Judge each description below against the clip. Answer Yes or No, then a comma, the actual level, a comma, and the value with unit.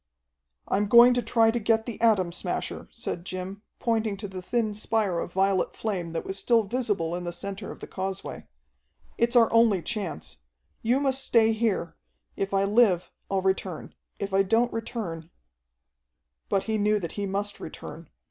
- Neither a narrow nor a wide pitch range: Yes, average, 3.3 semitones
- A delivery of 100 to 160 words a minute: No, average, 175 wpm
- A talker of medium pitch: No, high, 200 Hz